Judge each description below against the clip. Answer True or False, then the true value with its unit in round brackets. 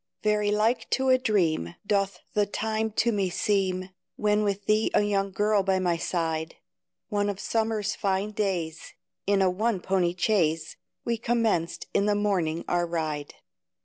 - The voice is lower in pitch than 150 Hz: False (200 Hz)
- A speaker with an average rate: True (160 wpm)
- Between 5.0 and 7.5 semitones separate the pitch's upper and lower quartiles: False (3.1 semitones)